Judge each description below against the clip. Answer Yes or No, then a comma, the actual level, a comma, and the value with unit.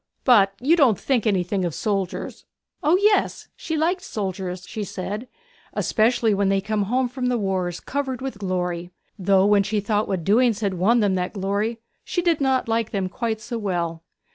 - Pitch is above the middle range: Yes, high, 210 Hz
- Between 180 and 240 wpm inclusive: Yes, average, 185 wpm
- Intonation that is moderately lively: Yes, average, 4.5 semitones